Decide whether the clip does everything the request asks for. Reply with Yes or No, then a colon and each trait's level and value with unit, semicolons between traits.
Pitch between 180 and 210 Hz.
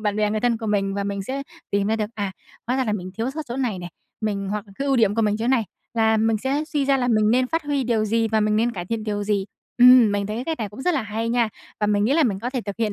No: high, 220 Hz